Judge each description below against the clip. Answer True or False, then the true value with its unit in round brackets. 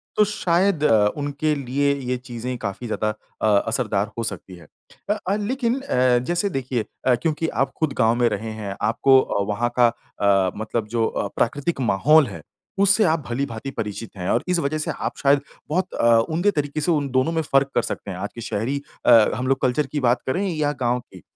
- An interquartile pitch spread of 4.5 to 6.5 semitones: True (5.1 semitones)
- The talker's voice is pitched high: False (130 Hz)